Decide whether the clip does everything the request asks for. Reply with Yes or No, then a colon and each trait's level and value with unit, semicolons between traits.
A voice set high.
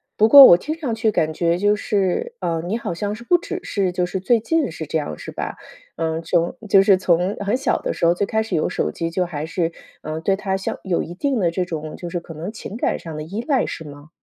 No: medium, 180 Hz